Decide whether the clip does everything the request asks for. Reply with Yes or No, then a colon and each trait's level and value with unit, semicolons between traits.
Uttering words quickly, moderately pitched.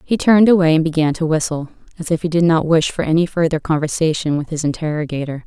Yes: fast, 220 wpm; medium, 160 Hz